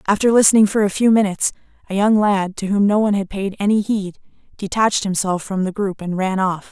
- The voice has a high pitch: Yes, high, 200 Hz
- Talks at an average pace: No, fast, 225 wpm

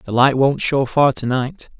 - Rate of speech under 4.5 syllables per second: Yes, 4.1 syllables/s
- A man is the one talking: Yes, male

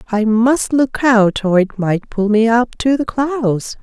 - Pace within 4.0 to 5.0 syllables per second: No, 3.7 syllables/s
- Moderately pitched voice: No, high, 230 Hz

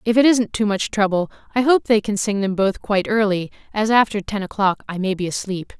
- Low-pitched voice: No, high, 205 Hz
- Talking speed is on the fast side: Yes, fast, 240 wpm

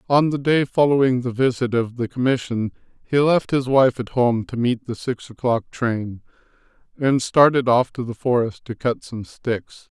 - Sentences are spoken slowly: No, average, 185 wpm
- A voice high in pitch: No, low, 125 Hz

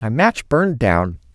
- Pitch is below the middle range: Yes, low, 130 Hz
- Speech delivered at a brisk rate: No, average, 180 wpm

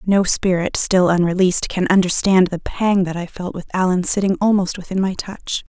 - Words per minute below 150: No, average, 190 wpm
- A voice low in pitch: No, medium, 185 Hz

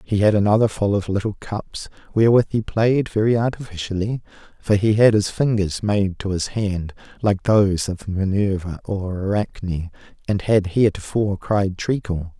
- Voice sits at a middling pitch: No, low, 100 Hz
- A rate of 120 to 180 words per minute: Yes, average, 155 wpm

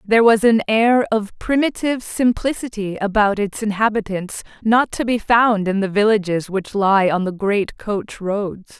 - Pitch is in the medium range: No, high, 210 Hz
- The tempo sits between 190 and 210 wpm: No, average, 165 wpm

